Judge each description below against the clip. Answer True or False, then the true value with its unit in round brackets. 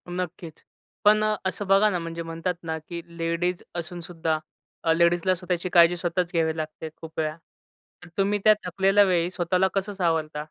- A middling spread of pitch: False (2.1 semitones)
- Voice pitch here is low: False (175 Hz)